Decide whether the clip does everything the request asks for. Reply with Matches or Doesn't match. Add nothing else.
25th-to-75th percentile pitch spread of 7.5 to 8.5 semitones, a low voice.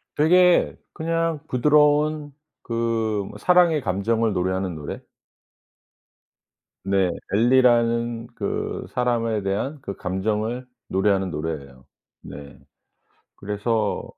Doesn't match